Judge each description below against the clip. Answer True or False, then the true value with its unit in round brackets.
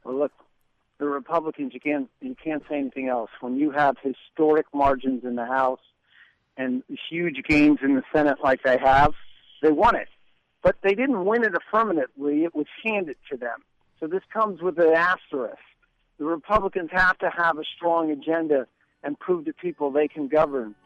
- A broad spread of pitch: False (4.3 semitones)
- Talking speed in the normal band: True (180 wpm)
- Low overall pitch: False (150 Hz)